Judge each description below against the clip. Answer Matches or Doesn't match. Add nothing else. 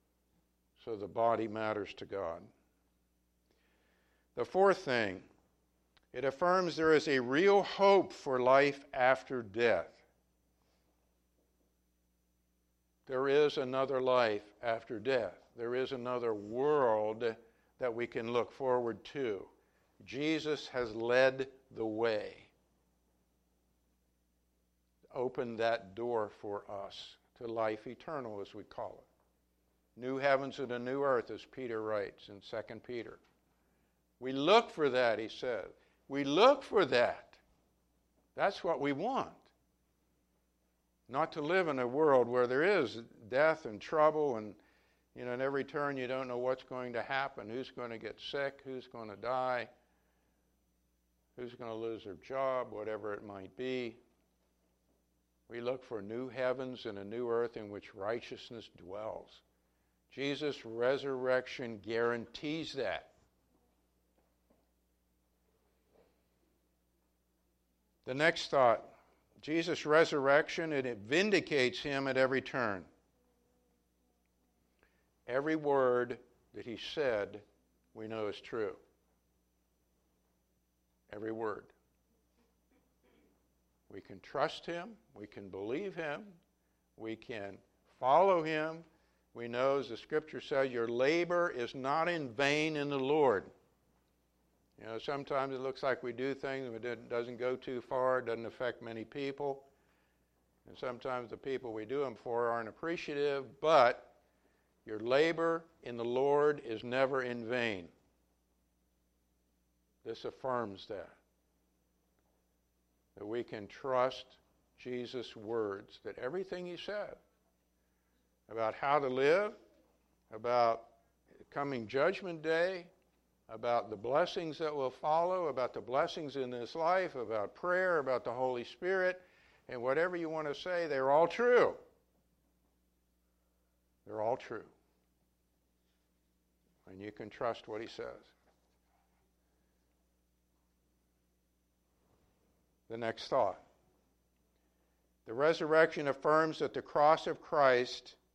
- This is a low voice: Matches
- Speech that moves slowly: Matches